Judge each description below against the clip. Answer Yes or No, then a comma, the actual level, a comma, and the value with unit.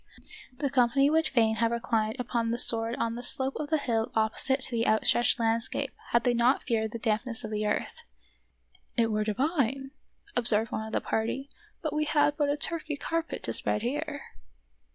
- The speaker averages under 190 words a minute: No, average, 195 wpm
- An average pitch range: Yes, average, 3.8 semitones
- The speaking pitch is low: No, high, 240 Hz